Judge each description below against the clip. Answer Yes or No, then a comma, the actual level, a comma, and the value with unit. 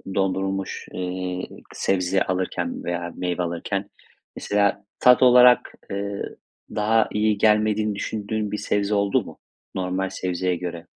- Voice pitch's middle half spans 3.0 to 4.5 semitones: No, narrow, 2.5 semitones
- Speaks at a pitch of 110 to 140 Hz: No, low, 100 Hz